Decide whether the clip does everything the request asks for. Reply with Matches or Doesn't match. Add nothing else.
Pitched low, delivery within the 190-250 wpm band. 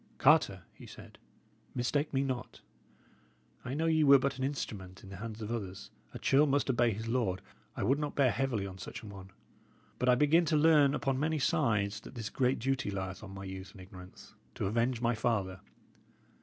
Matches